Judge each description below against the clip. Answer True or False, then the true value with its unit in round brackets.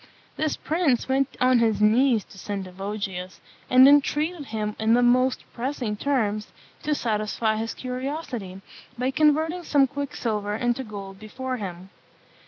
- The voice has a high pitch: True (240 Hz)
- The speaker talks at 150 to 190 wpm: False (135 wpm)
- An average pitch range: True (4.5 semitones)